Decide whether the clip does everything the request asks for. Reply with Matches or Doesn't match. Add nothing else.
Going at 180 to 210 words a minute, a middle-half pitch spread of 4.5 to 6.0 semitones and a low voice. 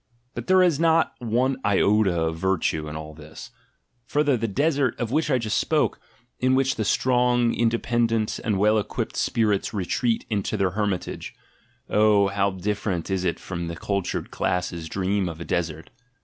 Doesn't match